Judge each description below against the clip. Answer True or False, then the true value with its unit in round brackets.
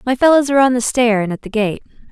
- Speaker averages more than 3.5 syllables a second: True (6.9 syllables/s)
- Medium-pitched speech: False (240 Hz)